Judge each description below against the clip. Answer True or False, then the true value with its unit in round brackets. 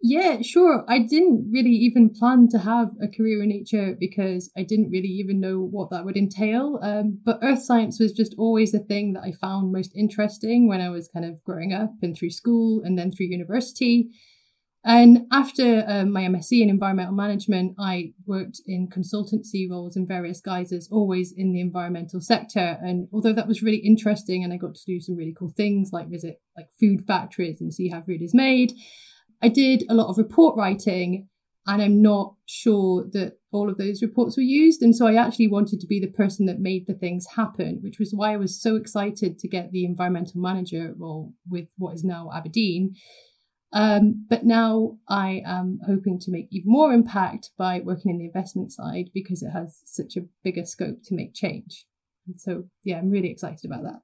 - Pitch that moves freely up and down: False (3.4 semitones)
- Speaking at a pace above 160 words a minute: True (205 wpm)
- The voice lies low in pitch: False (200 Hz)